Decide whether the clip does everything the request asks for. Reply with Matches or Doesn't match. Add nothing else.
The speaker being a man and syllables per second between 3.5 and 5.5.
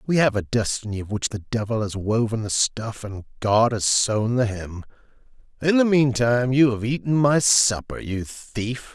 Matches